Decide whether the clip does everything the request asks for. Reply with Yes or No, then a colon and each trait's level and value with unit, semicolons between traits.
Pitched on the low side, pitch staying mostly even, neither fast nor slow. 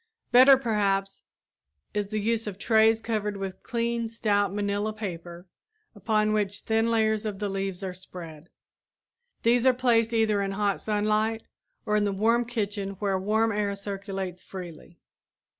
No: high, 210 Hz; narrow, 2.3 semitones; average, 150 wpm